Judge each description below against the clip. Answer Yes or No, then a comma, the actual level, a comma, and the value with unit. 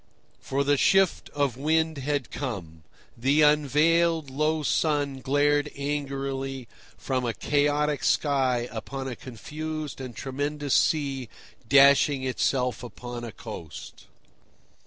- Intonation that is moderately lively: No, narrow, 2.3 semitones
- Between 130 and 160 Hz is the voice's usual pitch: Yes, medium, 140 Hz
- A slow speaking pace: Yes, slow, 115 wpm